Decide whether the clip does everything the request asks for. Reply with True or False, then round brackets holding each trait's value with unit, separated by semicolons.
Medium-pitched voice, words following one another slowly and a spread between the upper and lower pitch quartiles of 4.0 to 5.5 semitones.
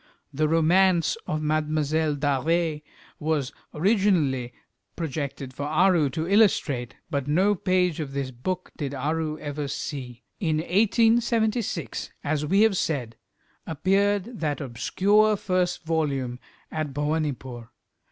True (155 Hz; 115 wpm; 4.6 semitones)